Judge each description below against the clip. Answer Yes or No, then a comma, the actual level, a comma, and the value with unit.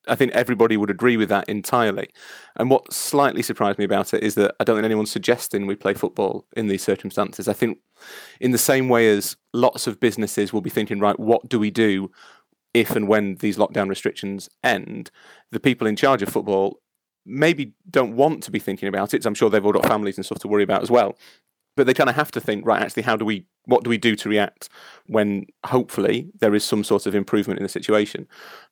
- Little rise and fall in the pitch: Yes, narrow, 2.3 semitones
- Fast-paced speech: Yes, fast, 230 wpm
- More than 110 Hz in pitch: No, low, 105 Hz